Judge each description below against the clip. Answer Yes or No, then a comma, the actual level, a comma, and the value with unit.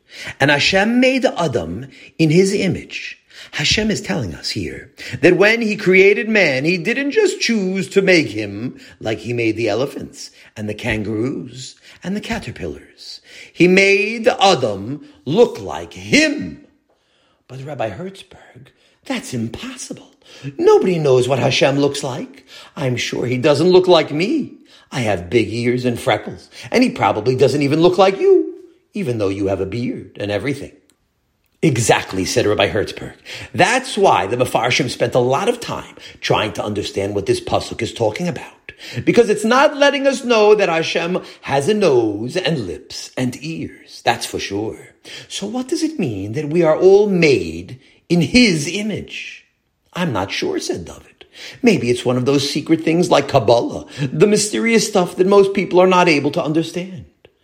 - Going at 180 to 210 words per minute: No, average, 165 wpm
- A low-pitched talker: No, medium, 180 Hz